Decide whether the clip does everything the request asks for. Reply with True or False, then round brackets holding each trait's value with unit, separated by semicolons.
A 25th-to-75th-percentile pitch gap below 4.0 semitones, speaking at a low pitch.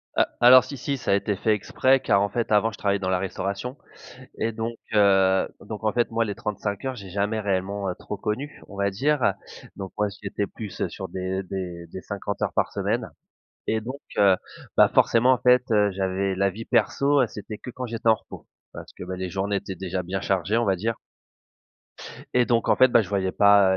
True (3.0 semitones; 100 Hz)